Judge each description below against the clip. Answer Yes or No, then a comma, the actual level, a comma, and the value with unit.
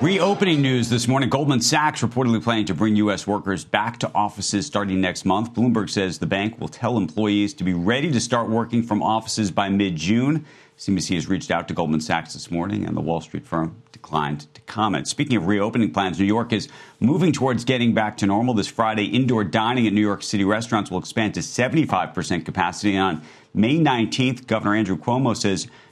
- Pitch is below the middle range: Yes, low, 105 Hz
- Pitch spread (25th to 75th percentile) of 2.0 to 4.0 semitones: Yes, average, 3.6 semitones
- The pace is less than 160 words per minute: No, average, 200 wpm